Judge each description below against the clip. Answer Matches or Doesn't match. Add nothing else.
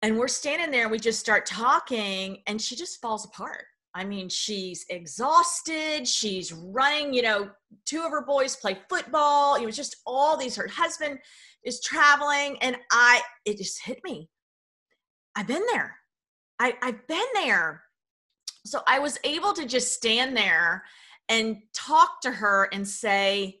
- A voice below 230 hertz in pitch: Doesn't match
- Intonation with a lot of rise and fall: Matches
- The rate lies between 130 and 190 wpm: Matches